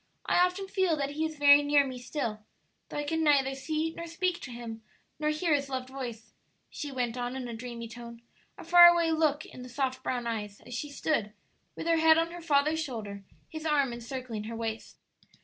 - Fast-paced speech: Yes, fast, 215 wpm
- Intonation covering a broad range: No, average, 4.9 semitones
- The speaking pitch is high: Yes, very high, 280 Hz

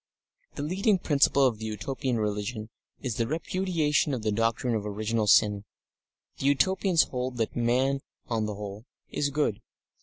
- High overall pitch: No, low, 120 Hz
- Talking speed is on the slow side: No, average, 155 wpm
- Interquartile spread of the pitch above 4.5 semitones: Yes, average, 4.9 semitones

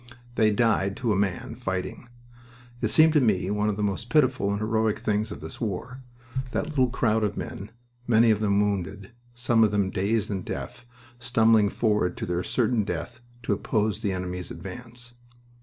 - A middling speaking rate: Yes, average, 180 wpm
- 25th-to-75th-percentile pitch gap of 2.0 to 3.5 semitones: Yes, average, 3.1 semitones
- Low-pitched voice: Yes, low, 105 Hz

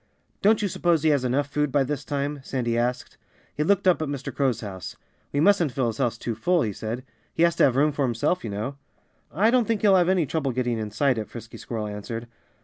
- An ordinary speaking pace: No, fast, 240 wpm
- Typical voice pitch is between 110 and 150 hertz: Yes, medium, 140 Hz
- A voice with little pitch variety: No, wide, 5.5 semitones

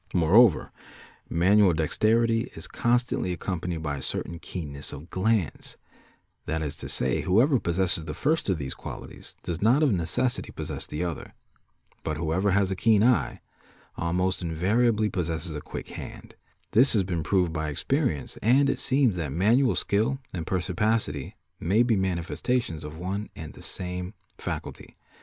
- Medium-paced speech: Yes, average, 155 wpm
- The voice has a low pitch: Yes, very low, 95 Hz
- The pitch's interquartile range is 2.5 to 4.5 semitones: No, wide, 5.5 semitones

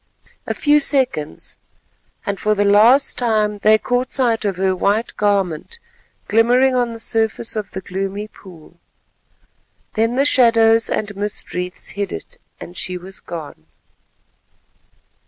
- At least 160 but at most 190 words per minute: No, slow, 135 wpm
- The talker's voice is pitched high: Yes, high, 210 Hz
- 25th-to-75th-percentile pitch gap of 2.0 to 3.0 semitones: No, average, 3.4 semitones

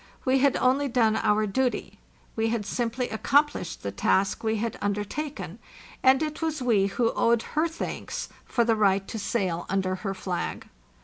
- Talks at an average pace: Yes, average, 170 wpm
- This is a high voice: Yes, high, 225 Hz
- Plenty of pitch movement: No, average, 4.7 semitones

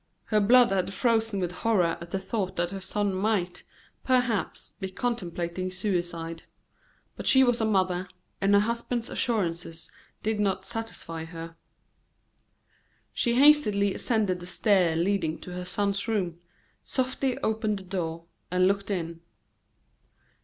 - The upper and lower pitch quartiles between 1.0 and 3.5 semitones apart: No, average, 3.9 semitones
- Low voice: No, high, 195 Hz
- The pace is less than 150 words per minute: Yes, average, 140 wpm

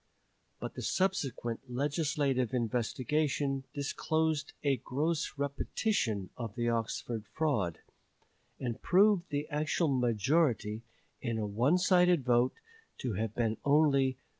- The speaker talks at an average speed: No, slow, 115 wpm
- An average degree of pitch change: Yes, average, 4.7 semitones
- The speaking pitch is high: No, low, 135 Hz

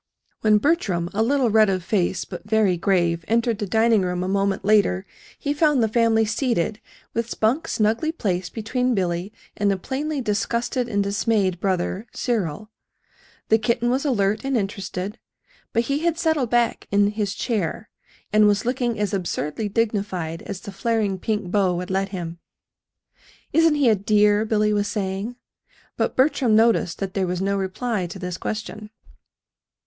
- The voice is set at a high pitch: Yes, high, 210 Hz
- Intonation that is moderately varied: Yes, average, 3.4 semitones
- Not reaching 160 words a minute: No, average, 165 wpm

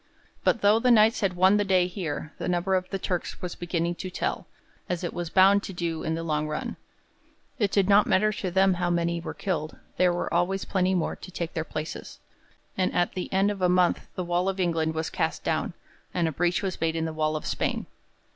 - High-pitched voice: No, medium, 180 Hz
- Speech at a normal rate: No, fast, 230 wpm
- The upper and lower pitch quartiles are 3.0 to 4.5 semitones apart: No, narrow, 2.4 semitones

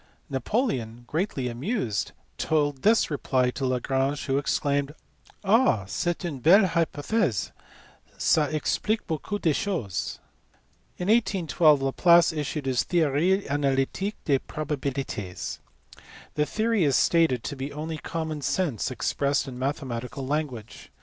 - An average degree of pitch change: Yes, average, 4.5 semitones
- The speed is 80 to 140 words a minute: Yes, slow, 135 wpm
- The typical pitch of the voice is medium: Yes, medium, 145 Hz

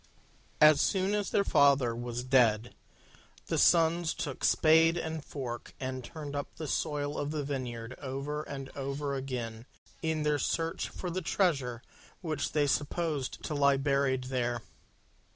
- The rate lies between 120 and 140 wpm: No, average, 150 wpm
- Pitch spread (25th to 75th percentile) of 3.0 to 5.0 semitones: Yes, average, 3.3 semitones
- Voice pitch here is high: No, medium, 140 Hz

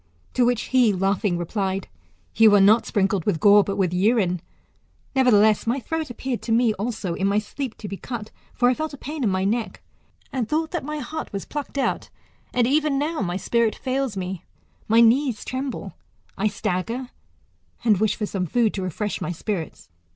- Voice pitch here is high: Yes, high, 220 Hz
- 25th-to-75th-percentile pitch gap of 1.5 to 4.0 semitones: No, average, 4.6 semitones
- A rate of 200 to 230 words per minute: No, average, 190 wpm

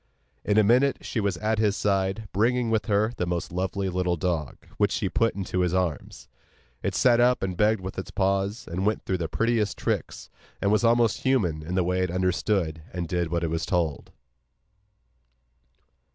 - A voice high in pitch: No, very low, 95 Hz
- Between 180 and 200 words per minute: Yes, average, 190 wpm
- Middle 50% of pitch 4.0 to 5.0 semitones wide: No, average, 3.6 semitones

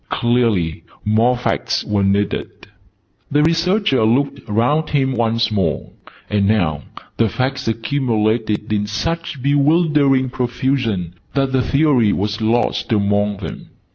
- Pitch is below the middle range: Yes, low, 120 Hz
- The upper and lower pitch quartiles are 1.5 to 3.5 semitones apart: No, average, 4.7 semitones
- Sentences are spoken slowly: Yes, slow, 120 wpm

